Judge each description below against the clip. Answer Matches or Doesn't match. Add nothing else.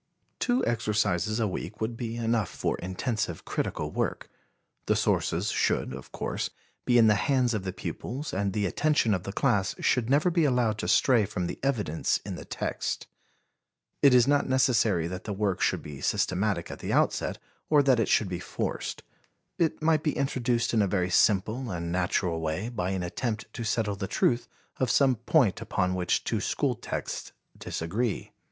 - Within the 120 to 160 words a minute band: Doesn't match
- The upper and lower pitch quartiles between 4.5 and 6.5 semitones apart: Matches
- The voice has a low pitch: Matches